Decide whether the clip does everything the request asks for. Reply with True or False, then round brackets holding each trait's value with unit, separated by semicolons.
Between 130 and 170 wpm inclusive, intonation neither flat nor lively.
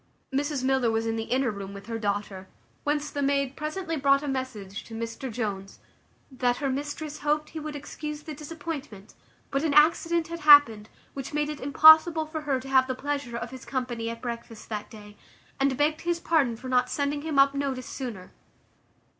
False (195 wpm; 4.4 semitones)